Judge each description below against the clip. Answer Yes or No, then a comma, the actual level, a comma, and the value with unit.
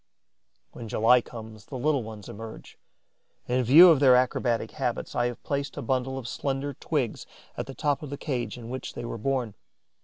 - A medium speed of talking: Yes, average, 190 wpm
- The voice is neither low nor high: No, low, 125 Hz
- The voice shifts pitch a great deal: No, average, 3.0 semitones